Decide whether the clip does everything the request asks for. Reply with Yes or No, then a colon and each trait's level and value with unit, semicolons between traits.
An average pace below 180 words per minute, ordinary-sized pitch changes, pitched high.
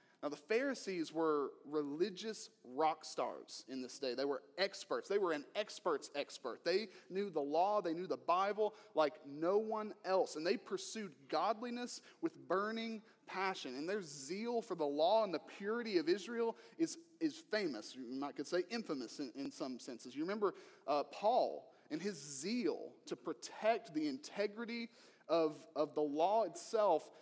No: average, 165 wpm; wide, 7.3 semitones; high, 210 Hz